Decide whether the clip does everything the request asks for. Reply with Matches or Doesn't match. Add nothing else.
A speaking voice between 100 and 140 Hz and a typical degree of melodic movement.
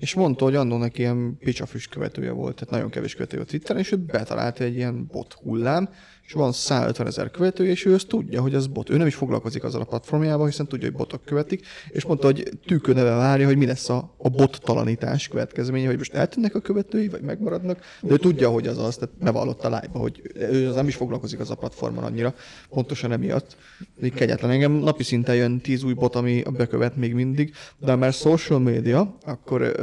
Matches